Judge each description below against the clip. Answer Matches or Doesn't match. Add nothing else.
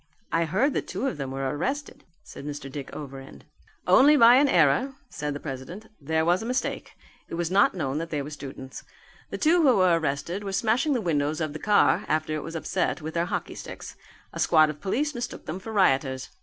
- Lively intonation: Matches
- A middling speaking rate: Doesn't match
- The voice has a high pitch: Doesn't match